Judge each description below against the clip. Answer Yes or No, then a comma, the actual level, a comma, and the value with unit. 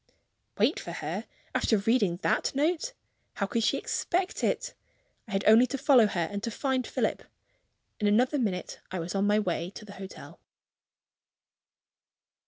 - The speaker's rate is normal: Yes, average, 160 wpm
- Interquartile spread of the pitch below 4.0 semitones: No, average, 5.0 semitones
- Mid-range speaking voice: No, high, 215 Hz